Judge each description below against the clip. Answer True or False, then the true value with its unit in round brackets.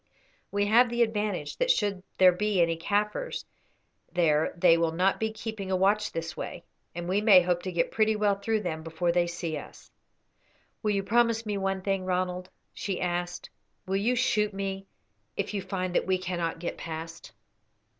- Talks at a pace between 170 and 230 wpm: True (185 wpm)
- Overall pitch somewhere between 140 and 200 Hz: True (190 Hz)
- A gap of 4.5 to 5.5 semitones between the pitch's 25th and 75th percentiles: False (3.3 semitones)